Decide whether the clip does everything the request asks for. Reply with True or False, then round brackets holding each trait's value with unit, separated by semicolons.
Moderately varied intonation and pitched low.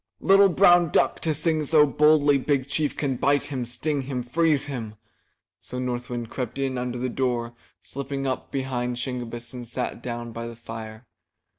True (3.1 semitones; 130 Hz)